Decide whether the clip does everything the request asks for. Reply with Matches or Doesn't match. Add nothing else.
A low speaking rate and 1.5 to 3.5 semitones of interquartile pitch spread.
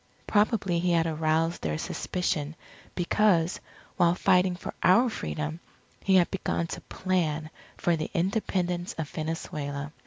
Matches